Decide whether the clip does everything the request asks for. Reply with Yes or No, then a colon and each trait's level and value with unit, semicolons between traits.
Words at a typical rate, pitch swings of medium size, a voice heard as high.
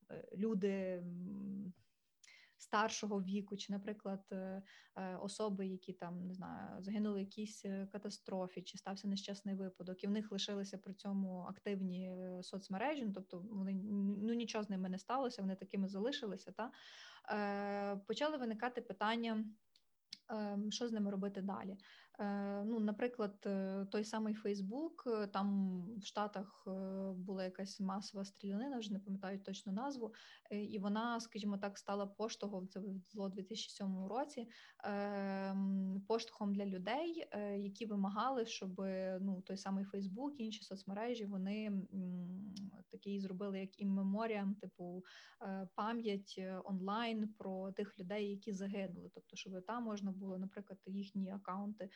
No: average, 125 wpm; narrow, 1.7 semitones; high, 200 Hz